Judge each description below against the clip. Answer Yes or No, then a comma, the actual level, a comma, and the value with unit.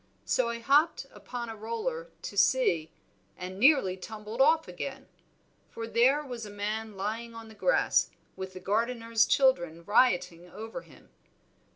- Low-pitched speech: No, high, 225 Hz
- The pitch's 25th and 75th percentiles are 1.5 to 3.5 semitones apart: No, average, 4.4 semitones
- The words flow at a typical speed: Yes, average, 150 wpm